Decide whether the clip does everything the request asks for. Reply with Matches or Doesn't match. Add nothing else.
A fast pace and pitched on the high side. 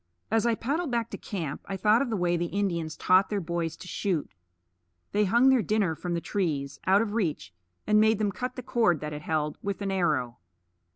Matches